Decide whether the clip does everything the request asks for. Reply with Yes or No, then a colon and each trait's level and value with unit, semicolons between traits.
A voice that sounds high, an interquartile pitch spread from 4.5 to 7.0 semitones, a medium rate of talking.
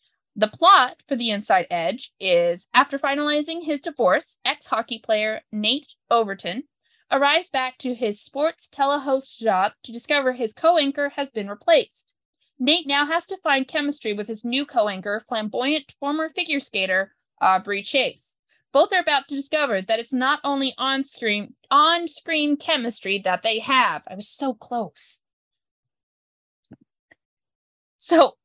Yes: very high, 265 Hz; average, 5.3 semitones; average, 145 wpm